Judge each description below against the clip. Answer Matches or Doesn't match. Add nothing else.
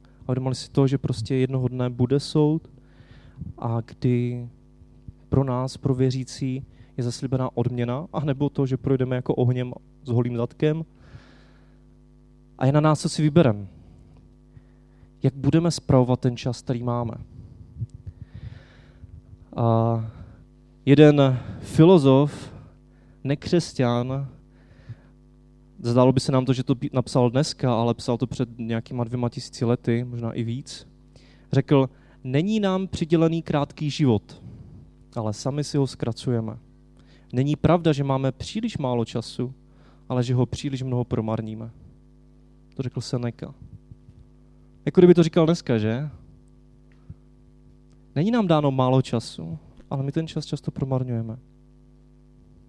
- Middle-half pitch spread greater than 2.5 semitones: Matches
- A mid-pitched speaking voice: Doesn't match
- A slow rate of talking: Doesn't match